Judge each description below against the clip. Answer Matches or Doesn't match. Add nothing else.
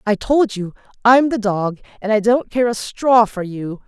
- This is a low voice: Doesn't match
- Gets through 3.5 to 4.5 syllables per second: Matches